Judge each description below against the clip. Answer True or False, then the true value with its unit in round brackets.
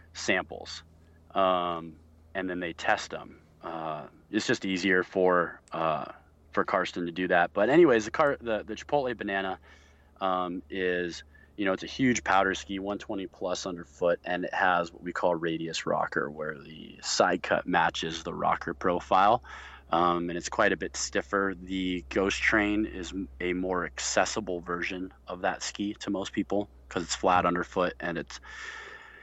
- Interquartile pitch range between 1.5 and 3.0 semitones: True (2.5 semitones)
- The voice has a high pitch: False (90 Hz)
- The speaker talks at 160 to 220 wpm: True (165 wpm)